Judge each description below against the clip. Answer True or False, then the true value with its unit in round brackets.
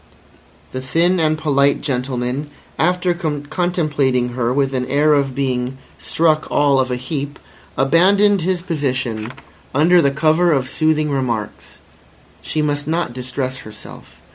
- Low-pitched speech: False (145 Hz)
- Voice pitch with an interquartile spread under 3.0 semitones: False (3.6 semitones)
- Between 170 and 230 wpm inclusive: False (135 wpm)